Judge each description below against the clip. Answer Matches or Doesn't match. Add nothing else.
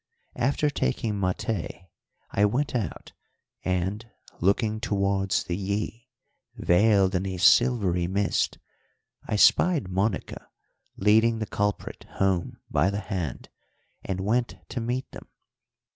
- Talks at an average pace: Doesn't match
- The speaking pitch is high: Doesn't match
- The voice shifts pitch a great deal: Doesn't match